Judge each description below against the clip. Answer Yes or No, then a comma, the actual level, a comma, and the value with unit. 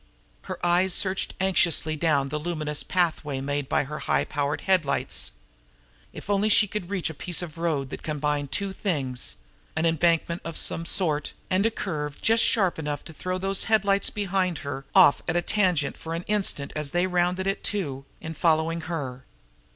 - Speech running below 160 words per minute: No, average, 175 wpm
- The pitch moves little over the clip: No, average, 4.1 semitones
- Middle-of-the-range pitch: Yes, medium, 170 Hz